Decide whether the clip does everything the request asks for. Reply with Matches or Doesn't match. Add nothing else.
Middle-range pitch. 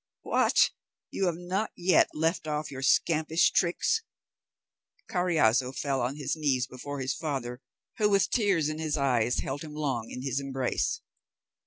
Matches